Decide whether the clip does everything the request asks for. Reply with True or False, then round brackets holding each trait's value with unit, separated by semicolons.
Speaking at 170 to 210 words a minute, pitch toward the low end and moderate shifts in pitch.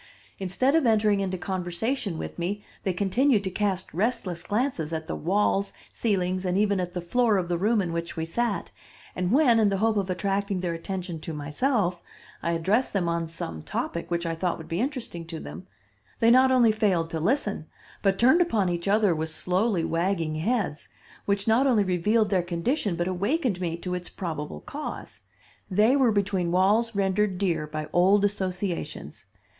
False (185 wpm; 190 Hz; 3.9 semitones)